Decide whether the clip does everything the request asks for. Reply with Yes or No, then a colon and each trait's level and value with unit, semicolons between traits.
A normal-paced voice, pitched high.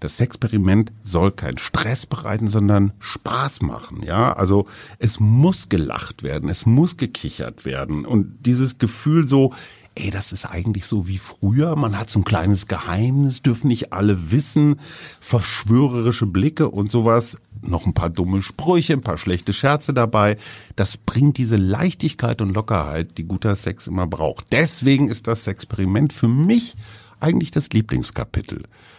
No: average, 155 wpm; low, 110 Hz